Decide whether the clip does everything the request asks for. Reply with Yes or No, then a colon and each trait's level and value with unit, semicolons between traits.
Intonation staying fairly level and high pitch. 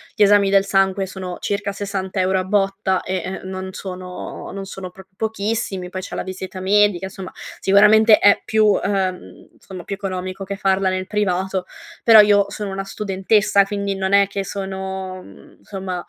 Yes: narrow, 1.3 semitones; high, 195 Hz